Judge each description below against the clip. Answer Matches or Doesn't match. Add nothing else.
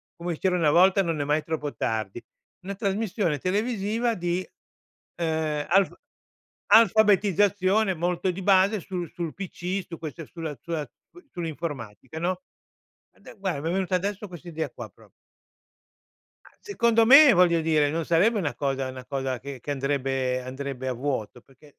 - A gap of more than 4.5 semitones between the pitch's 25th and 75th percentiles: Matches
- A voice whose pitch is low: Doesn't match